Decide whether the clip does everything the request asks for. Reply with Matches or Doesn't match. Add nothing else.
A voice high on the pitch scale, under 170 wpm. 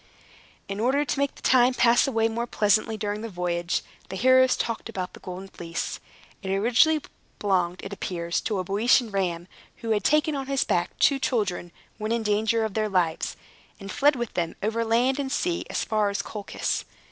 Doesn't match